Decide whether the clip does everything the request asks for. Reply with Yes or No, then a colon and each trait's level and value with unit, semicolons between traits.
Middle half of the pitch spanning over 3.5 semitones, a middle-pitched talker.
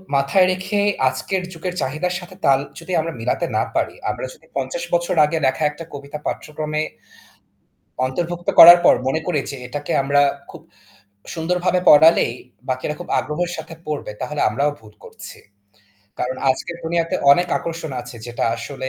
Yes: average, 4.1 semitones; medium, 155 Hz